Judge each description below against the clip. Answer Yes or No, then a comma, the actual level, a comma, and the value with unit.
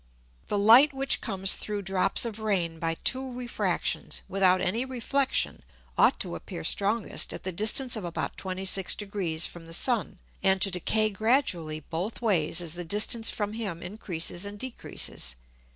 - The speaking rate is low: No, average, 160 wpm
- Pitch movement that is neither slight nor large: Yes, average, 4.3 semitones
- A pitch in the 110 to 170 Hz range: No, high, 200 Hz